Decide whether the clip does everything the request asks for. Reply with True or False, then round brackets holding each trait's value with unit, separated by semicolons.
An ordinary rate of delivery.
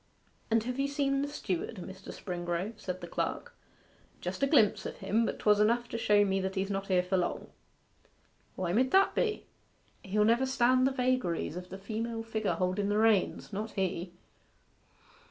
True (185 wpm)